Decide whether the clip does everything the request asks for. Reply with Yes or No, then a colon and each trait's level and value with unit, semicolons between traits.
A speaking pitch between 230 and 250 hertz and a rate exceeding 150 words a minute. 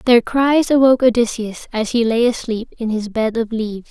Yes: high, 235 Hz; average, 200 wpm